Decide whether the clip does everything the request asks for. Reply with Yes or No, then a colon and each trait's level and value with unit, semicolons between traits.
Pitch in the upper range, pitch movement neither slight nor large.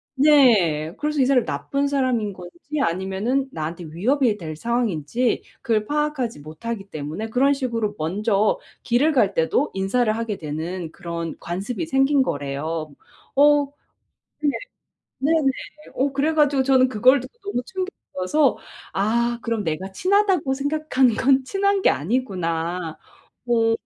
No: high, 235 Hz; wide, 7.1 semitones